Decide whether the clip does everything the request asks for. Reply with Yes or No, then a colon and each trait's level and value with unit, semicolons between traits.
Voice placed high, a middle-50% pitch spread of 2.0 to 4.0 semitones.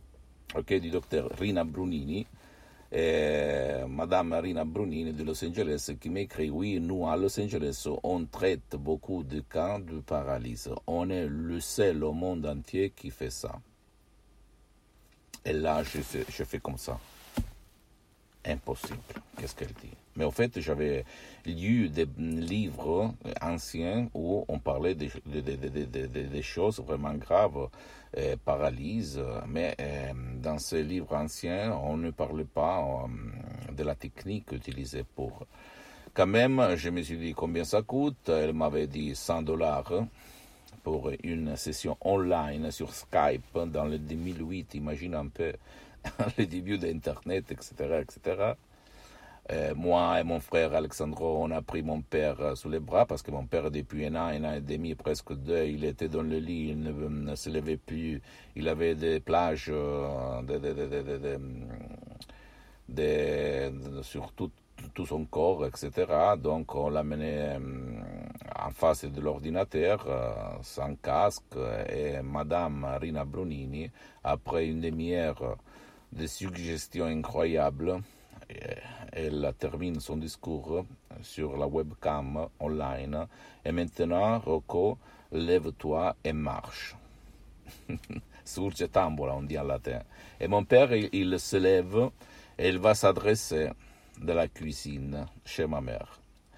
No: very low, 80 Hz; narrow, 2.5 semitones